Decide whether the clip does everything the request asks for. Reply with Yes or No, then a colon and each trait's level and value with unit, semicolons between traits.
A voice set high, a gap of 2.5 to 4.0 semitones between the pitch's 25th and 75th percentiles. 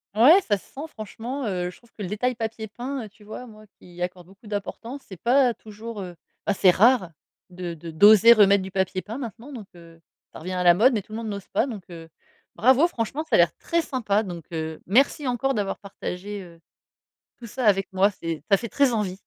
No: high, 210 Hz; average, 4.5 semitones